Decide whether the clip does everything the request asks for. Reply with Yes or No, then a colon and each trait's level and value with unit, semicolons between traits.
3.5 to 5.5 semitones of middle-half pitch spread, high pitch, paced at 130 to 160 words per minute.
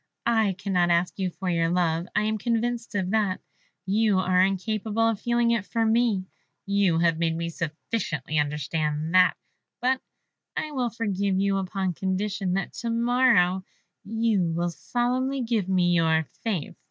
Yes: average, 4.5 semitones; high, 195 Hz; average, 155 wpm